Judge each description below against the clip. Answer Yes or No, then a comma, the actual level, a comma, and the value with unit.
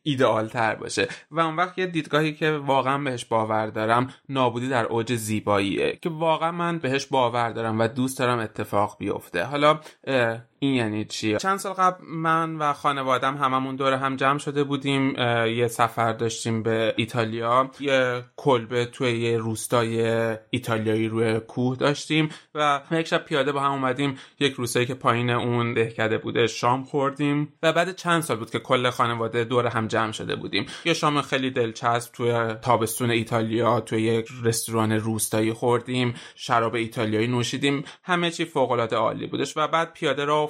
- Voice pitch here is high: No, low, 125 Hz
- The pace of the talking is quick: Yes, fast, 165 wpm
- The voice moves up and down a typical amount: Yes, average, 3.8 semitones